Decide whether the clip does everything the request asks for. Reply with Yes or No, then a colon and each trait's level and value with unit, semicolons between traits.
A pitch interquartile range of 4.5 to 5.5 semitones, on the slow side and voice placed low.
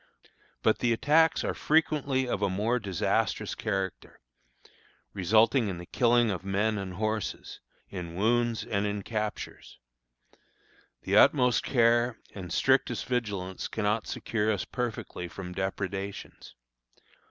No: average, 3.6 semitones; slow, 120 wpm; low, 105 Hz